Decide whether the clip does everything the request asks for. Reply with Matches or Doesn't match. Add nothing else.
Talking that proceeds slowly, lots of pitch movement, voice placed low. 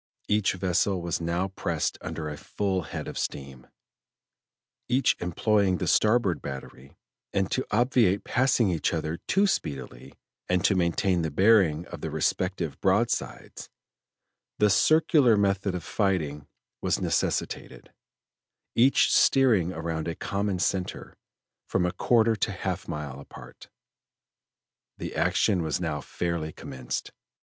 Doesn't match